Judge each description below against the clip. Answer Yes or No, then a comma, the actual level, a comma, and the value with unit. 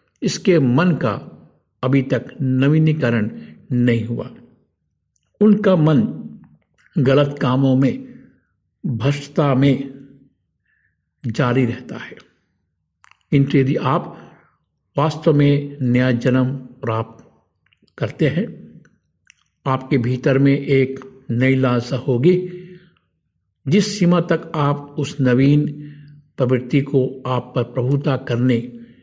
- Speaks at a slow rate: Yes, slow, 95 wpm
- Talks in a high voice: No, low, 135 Hz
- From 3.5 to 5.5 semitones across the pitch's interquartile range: No, average, 2.7 semitones